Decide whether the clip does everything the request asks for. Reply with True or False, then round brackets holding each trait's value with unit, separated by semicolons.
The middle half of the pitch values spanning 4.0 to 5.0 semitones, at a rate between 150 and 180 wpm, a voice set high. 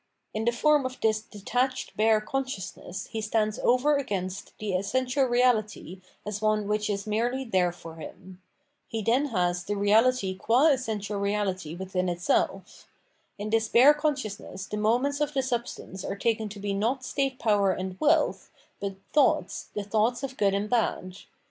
True (4.3 semitones; 165 wpm; 215 Hz)